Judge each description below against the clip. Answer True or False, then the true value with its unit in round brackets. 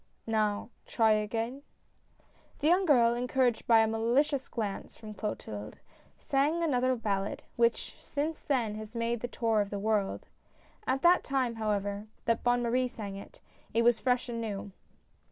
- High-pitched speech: True (230 Hz)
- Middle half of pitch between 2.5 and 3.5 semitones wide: True (3.1 semitones)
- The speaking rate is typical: True (165 wpm)